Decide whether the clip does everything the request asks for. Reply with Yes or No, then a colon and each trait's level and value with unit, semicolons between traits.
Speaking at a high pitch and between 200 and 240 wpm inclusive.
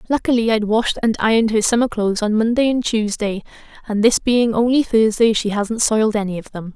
Yes: high, 220 Hz; fast, 205 wpm